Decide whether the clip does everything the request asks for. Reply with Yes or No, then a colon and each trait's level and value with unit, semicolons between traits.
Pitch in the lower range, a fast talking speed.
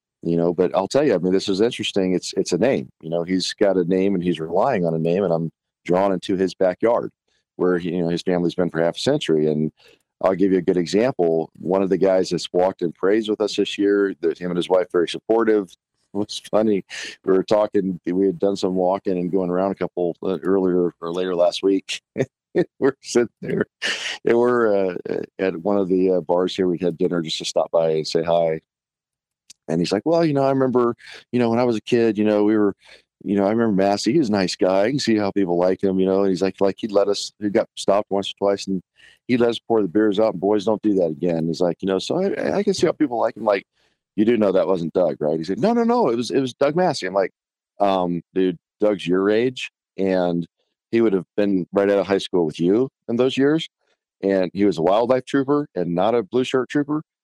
Yes: very low, 95 Hz; fast, 255 wpm